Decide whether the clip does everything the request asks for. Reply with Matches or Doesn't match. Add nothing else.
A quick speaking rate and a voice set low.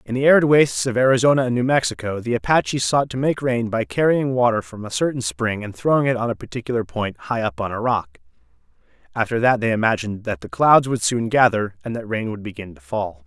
Matches